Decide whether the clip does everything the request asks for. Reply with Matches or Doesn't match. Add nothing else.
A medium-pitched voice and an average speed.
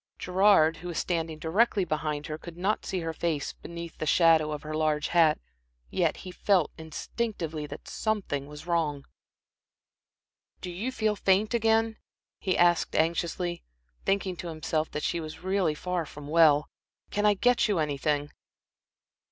Matches